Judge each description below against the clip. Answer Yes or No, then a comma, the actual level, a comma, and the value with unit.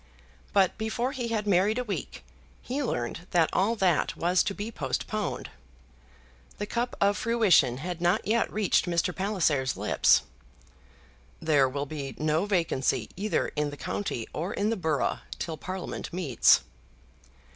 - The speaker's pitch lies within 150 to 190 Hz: Yes, medium, 185 Hz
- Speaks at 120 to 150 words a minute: Yes, average, 145 wpm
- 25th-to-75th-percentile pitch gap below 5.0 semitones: No, average, 5.3 semitones